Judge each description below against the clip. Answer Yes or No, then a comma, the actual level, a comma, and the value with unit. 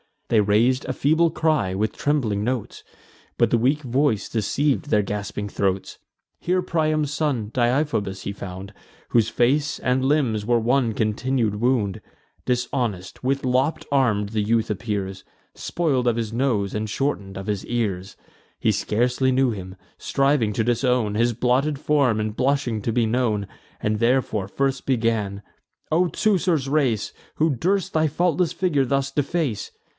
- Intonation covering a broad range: No, average, 4.8 semitones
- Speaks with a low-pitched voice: Yes, low, 120 Hz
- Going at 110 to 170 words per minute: Yes, average, 150 wpm